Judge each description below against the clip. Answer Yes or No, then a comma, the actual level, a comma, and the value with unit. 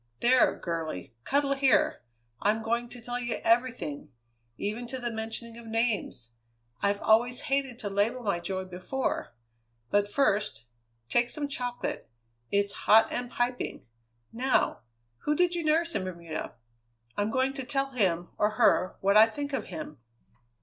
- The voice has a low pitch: No, high, 230 Hz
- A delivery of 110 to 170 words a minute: Yes, average, 150 wpm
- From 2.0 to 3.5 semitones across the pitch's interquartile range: No, average, 4.3 semitones